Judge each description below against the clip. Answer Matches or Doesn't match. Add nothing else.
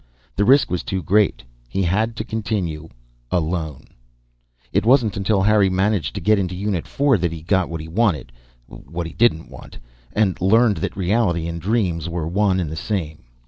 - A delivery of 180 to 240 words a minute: Matches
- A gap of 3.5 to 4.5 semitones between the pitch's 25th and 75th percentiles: Matches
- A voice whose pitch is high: Doesn't match